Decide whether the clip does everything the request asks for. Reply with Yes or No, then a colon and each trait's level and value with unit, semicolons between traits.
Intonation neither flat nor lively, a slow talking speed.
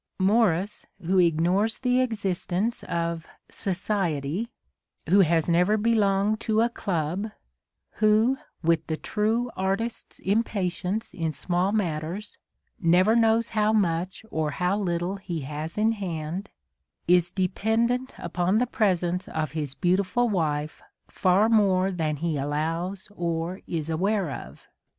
Yes: average, 4.3 semitones; slow, 125 wpm